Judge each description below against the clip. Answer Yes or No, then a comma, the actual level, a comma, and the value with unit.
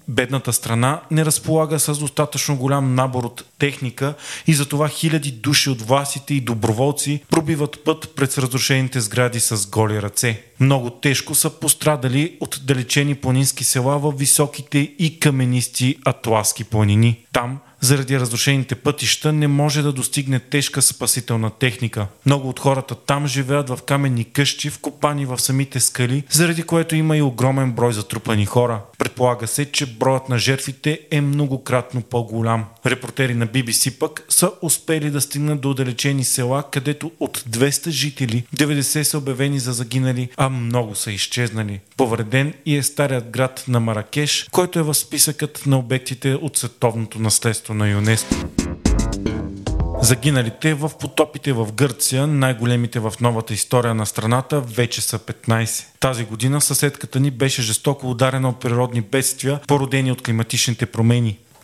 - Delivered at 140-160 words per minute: Yes, average, 145 wpm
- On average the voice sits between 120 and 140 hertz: Yes, low, 135 Hz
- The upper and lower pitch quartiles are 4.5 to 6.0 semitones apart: No, average, 3.3 semitones